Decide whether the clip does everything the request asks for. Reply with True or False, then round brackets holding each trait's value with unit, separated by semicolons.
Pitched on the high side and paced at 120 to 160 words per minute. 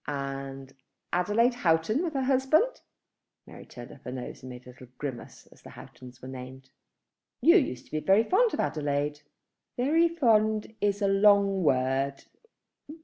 False (175 Hz; 155 wpm)